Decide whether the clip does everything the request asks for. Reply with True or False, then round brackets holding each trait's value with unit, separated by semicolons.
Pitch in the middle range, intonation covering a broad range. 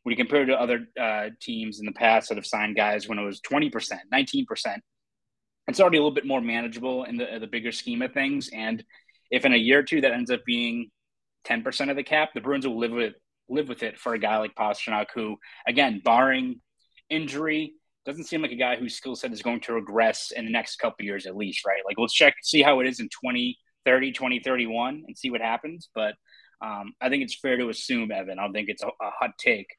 False (130 Hz; 5.7 semitones)